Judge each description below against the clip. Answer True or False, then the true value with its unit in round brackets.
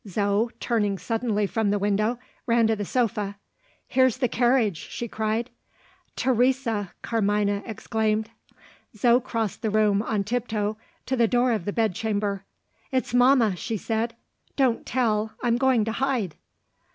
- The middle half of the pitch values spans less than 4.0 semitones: True (2.7 semitones)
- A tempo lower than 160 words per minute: True (145 wpm)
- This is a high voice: True (225 Hz)